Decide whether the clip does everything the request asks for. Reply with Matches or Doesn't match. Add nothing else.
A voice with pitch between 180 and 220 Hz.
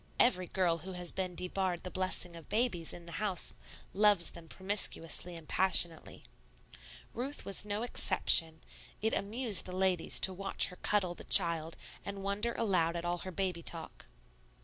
Matches